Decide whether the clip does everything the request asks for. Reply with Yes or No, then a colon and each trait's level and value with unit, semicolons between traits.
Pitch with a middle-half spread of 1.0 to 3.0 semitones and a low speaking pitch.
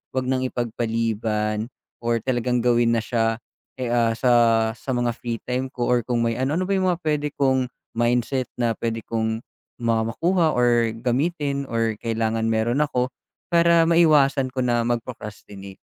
Yes: narrow, 2.6 semitones; low, 120 Hz